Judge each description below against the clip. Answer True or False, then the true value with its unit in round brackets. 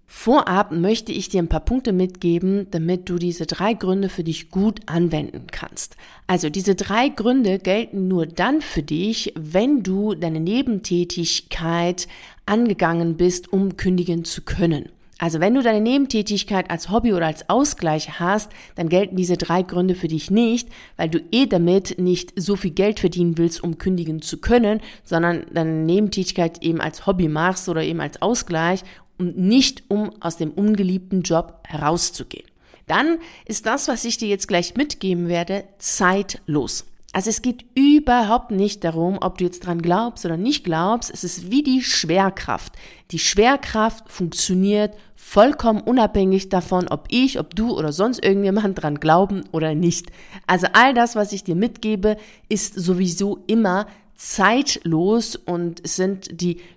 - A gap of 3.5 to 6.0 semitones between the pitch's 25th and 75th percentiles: True (3.8 semitones)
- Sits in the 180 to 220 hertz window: True (185 Hz)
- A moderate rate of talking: True (160 wpm)